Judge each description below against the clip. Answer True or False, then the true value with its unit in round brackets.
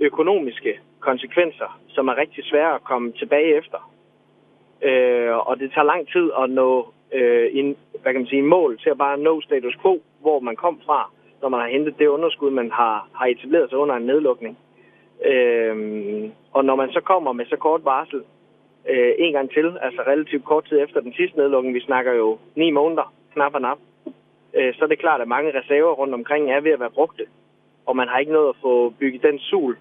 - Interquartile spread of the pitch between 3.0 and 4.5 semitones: False (5.2 semitones)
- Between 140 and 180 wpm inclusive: False (210 wpm)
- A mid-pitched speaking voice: True (145 Hz)